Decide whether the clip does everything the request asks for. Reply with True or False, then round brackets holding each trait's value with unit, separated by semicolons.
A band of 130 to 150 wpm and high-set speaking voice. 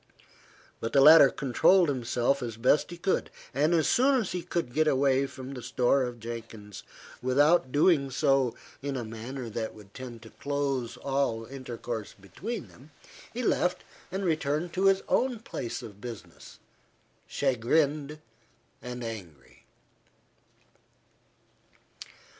False (135 wpm; 135 Hz)